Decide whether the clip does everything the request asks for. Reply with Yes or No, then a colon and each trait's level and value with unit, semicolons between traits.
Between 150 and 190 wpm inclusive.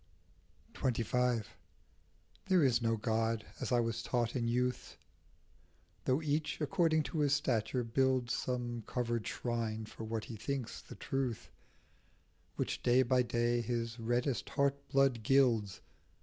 No: average, 140 wpm